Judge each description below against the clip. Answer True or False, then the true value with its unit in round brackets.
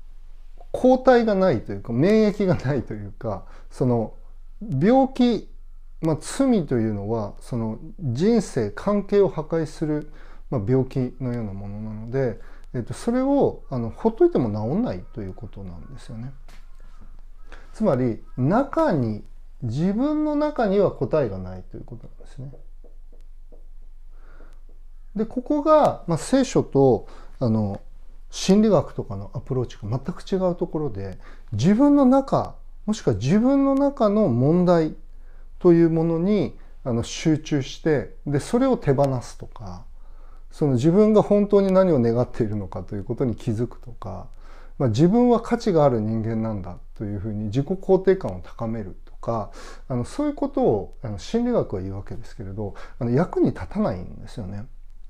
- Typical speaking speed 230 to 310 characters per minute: True (285 characters per minute)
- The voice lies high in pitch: False (130 Hz)